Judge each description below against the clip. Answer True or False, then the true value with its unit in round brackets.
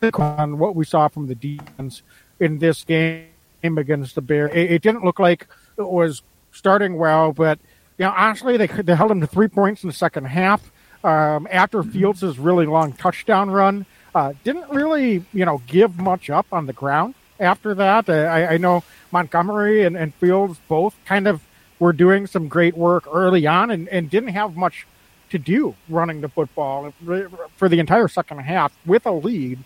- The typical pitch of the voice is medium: True (175 Hz)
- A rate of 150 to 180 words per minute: False (190 wpm)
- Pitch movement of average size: True (3.8 semitones)